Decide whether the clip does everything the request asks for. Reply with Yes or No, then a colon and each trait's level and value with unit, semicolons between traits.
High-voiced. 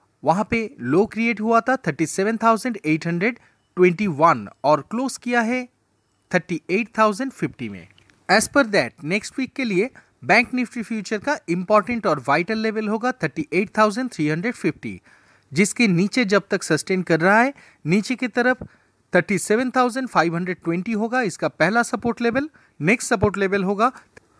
Yes: high, 210 Hz